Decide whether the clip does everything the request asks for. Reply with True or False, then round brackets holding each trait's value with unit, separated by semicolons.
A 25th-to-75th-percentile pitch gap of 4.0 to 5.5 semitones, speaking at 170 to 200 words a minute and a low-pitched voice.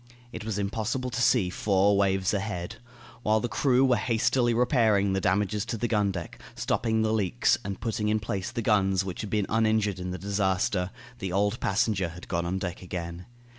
False (2.8 semitones; 195 wpm; 100 Hz)